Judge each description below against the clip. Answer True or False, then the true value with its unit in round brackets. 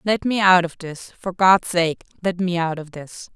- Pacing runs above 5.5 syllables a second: False (4.5 syllables/s)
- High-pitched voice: False (180 Hz)